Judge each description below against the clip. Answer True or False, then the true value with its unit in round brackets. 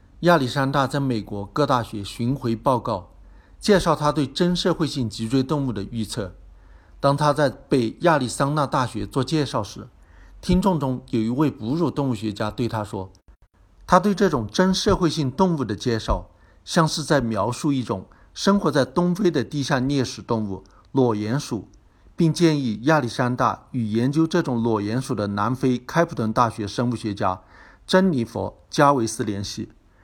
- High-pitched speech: False (125 Hz)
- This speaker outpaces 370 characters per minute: False (255 characters per minute)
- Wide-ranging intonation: True (5.8 semitones)